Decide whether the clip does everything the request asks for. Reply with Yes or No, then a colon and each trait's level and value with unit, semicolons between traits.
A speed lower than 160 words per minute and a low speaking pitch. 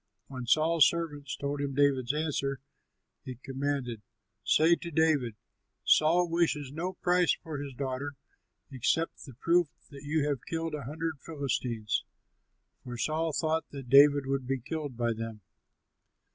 No: average, 145 wpm; medium, 145 Hz